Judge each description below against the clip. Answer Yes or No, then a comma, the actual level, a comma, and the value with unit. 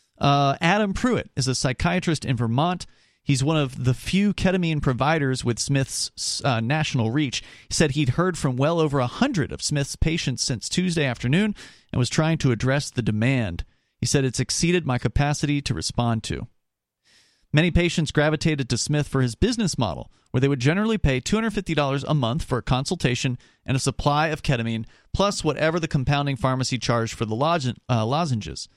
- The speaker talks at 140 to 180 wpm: No, average, 190 wpm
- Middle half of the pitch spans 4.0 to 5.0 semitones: Yes, average, 4.3 semitones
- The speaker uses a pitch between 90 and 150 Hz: Yes, medium, 140 Hz